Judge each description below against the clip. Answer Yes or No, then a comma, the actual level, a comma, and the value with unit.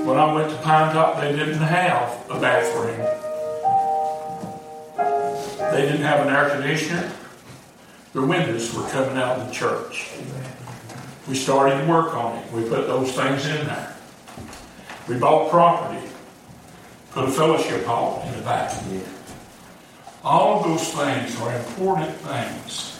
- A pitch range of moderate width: Yes, average, 3.5 semitones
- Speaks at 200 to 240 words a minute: No, average, 140 wpm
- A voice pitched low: No, medium, 145 Hz